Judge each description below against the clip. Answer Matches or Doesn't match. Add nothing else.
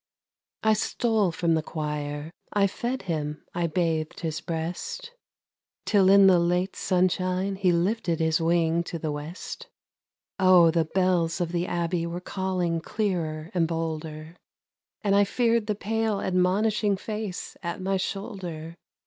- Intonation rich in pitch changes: Doesn't match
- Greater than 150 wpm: Doesn't match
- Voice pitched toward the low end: Doesn't match